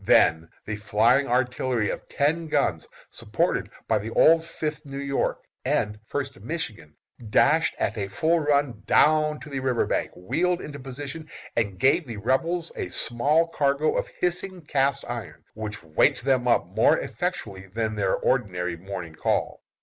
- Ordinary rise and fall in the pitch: No, wide, 6.4 semitones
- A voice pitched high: No, low, 130 Hz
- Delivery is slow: No, average, 155 wpm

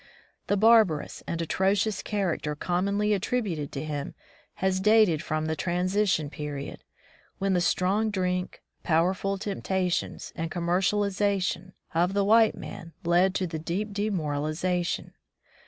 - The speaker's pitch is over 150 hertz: Yes, medium, 185 Hz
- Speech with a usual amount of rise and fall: Yes, average, 3.4 semitones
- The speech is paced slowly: Yes, slow, 125 wpm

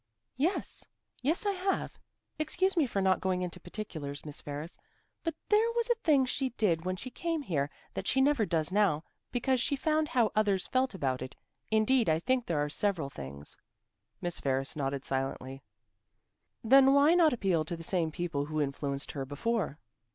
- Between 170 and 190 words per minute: Yes, average, 180 wpm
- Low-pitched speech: No, high, 190 Hz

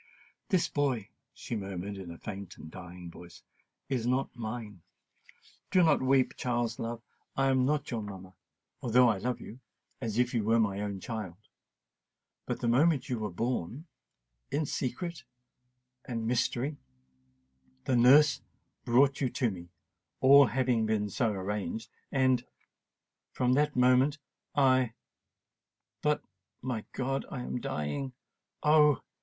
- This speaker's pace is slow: Yes, slow, 115 wpm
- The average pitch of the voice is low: Yes, low, 120 Hz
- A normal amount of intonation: Yes, average, 4.4 semitones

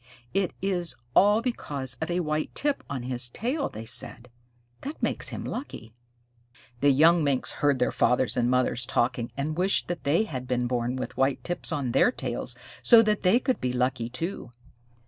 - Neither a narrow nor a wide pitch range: No, wide, 6.6 semitones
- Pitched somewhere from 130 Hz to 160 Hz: Yes, medium, 140 Hz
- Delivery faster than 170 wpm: Yes, average, 185 wpm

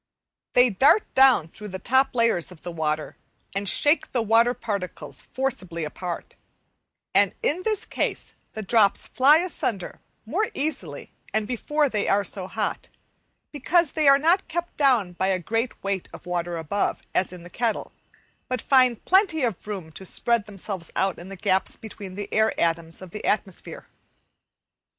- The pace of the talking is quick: No, average, 165 wpm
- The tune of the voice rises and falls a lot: Yes, wide, 6.3 semitones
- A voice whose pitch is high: Yes, high, 210 Hz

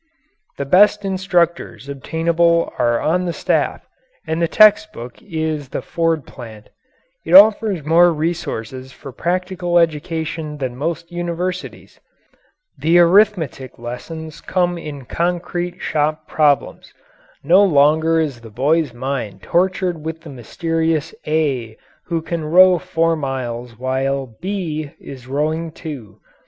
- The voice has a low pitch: No, medium, 160 Hz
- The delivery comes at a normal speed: No, slow, 125 wpm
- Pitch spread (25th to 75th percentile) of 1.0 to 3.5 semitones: No, average, 4.1 semitones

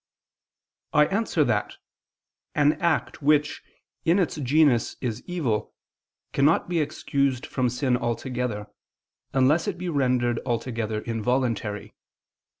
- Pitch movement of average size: Yes, average, 4.3 semitones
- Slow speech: Yes, slow, 110 wpm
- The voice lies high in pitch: No, low, 130 Hz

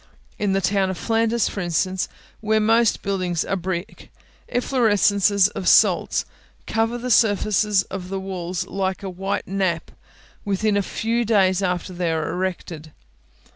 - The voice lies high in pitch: Yes, high, 195 Hz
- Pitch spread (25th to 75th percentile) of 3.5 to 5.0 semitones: No, narrow, 2.6 semitones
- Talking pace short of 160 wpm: Yes, average, 150 wpm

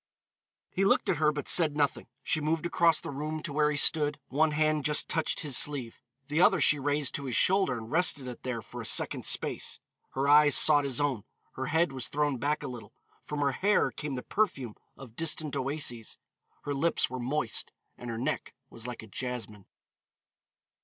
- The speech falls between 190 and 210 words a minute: Yes, average, 200 wpm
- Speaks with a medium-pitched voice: Yes, medium, 145 Hz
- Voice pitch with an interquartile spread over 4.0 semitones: No, average, 3.2 semitones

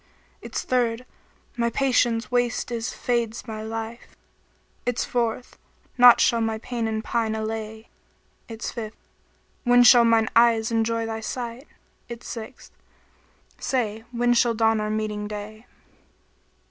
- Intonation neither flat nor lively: No, narrow, 1.6 semitones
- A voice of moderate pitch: No, high, 230 Hz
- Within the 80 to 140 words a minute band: Yes, slow, 135 wpm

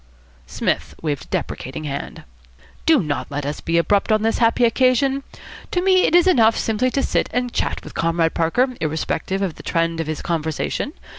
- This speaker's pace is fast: No, average, 190 wpm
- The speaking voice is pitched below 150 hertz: No, high, 195 Hz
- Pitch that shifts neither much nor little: No, wide, 7.9 semitones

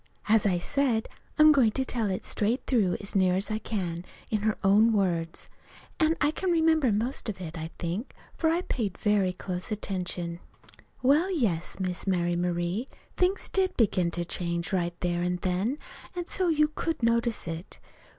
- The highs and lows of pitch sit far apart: Yes, wide, 6.8 semitones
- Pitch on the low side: No, high, 205 Hz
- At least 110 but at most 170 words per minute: No, average, 180 wpm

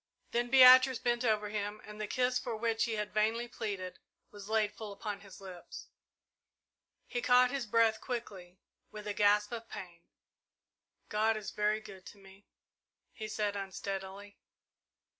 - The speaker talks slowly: No, average, 155 wpm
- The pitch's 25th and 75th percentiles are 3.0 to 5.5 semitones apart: No, narrow, 2.5 semitones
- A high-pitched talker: Yes, high, 215 Hz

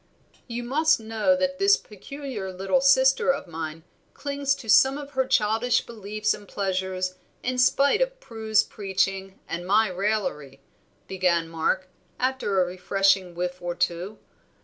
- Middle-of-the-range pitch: No, high, 210 Hz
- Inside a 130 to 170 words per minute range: Yes, average, 145 wpm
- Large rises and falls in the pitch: Yes, wide, 6.1 semitones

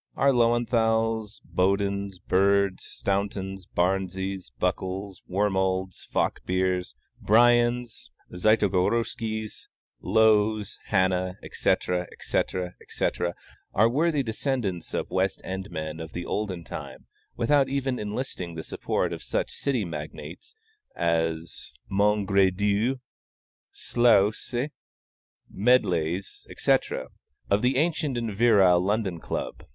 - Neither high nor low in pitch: No, low, 100 Hz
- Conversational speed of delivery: No, slow, 100 wpm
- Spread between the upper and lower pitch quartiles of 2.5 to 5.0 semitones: Yes, average, 3.8 semitones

